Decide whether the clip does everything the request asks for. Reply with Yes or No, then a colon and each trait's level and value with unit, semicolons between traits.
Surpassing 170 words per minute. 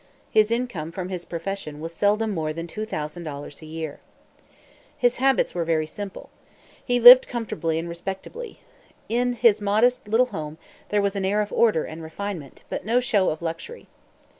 No: average, 165 wpm